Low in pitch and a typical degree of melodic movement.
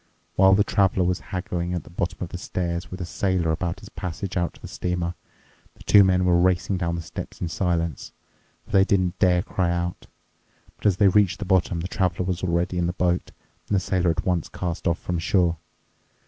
No: very low, 90 Hz; narrow, 1.4 semitones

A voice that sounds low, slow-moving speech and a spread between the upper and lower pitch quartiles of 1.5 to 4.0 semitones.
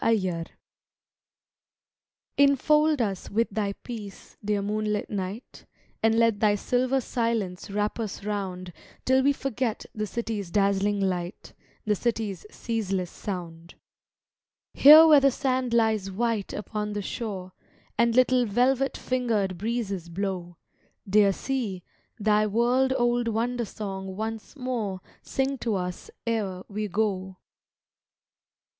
No: high, 215 Hz; slow, 125 wpm; average, 3.6 semitones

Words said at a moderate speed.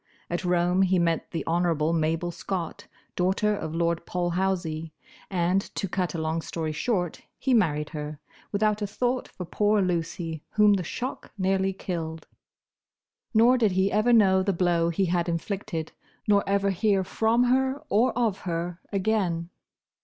Yes: average, 155 wpm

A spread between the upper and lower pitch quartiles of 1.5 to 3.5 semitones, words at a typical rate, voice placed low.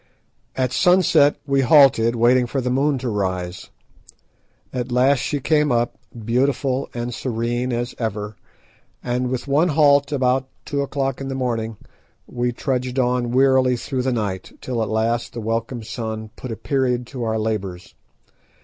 Yes: average, 2.7 semitones; average, 160 wpm; low, 125 Hz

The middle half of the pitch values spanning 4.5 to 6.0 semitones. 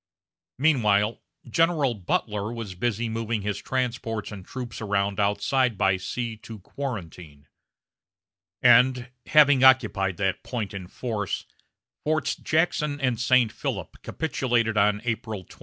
No: average, 4.1 semitones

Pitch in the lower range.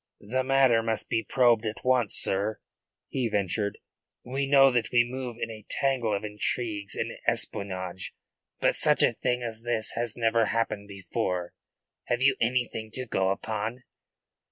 Yes: low, 115 Hz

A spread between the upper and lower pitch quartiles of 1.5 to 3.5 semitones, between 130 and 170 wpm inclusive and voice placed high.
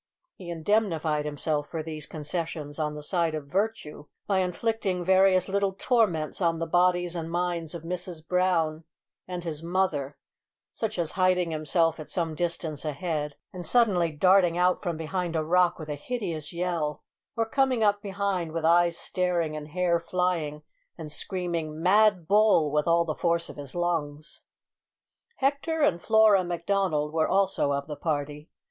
No: average, 3.0 semitones; average, 160 wpm; medium, 170 Hz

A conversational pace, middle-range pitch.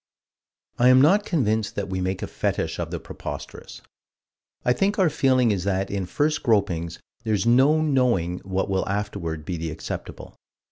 No: average, 170 wpm; low, 105 Hz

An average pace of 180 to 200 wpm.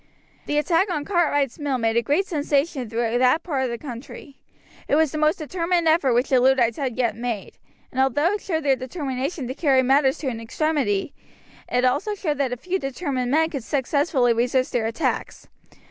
Yes: average, 195 wpm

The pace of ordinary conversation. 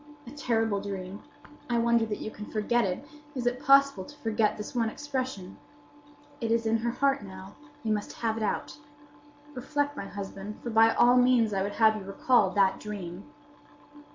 Yes: average, 180 wpm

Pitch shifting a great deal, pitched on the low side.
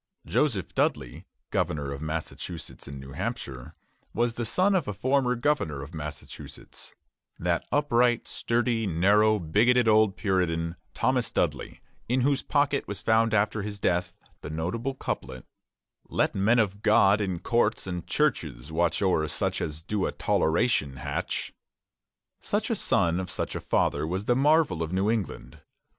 Yes: wide, 6.5 semitones; low, 100 Hz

